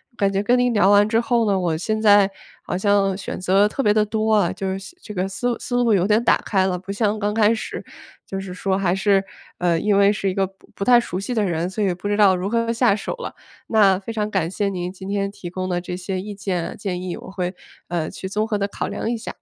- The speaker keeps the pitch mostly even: Yes, narrow, 2.3 semitones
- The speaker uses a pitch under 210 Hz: Yes, high, 200 Hz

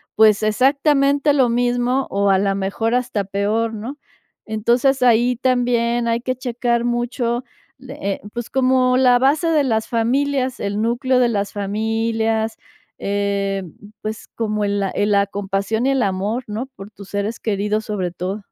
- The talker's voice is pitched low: No, high, 230 Hz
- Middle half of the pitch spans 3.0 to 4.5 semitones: Yes, average, 3.6 semitones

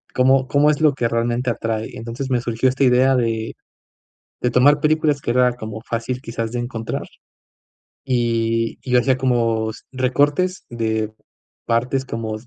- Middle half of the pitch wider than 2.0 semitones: Yes, narrow, 2.5 semitones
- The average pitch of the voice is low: Yes, low, 125 Hz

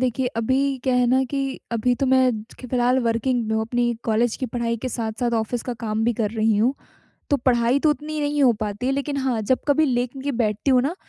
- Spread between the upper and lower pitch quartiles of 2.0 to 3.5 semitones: Yes, narrow, 2.5 semitones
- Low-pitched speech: No, very high, 250 Hz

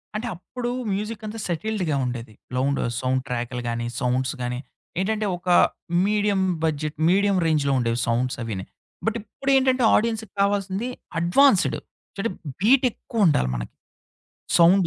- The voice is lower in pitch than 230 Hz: Yes, medium, 185 Hz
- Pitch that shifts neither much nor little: No, wide, 9.0 semitones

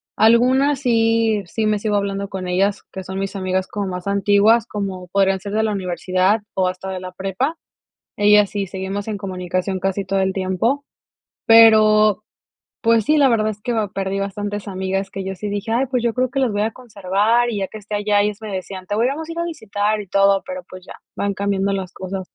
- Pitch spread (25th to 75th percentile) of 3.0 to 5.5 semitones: No, narrow, 2.5 semitones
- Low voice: No, high, 200 Hz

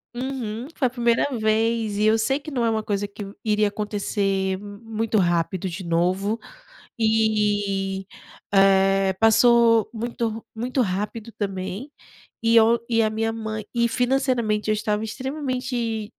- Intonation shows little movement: Yes, narrow, 2.3 semitones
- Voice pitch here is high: Yes, high, 220 Hz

